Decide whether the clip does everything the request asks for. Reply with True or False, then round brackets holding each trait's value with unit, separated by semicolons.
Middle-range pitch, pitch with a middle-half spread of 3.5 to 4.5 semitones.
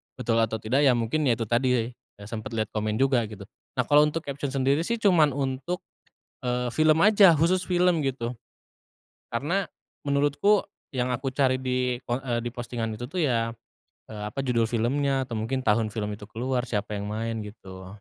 False (125 Hz; 3.9 semitones)